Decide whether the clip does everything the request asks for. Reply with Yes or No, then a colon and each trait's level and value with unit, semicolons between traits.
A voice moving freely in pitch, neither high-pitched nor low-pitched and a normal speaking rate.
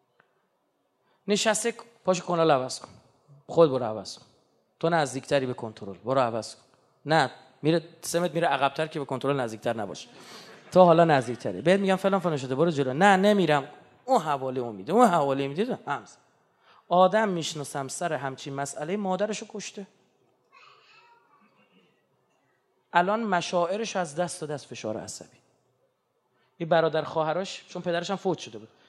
Yes: wide, 5.9 semitones; medium, 165 Hz; average, 145 wpm